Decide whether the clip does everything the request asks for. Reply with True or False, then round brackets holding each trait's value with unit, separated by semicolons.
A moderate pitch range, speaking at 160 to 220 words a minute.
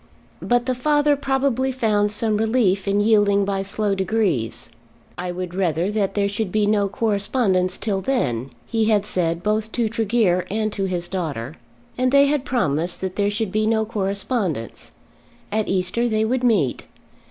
True (3.4 semitones; 165 wpm)